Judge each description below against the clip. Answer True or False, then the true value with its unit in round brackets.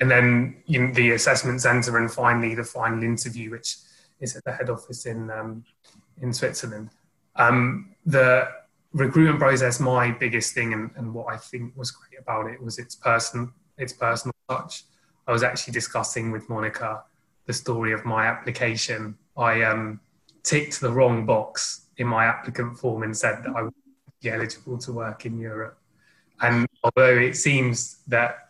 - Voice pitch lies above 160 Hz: False (120 Hz)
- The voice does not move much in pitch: True (1.8 semitones)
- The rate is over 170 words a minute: False (165 wpm)